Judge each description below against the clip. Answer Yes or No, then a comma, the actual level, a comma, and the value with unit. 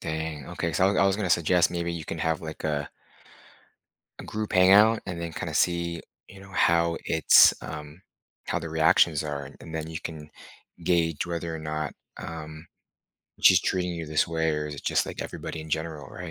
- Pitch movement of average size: No, narrow, 1.8 semitones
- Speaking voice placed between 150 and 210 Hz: No, very low, 80 Hz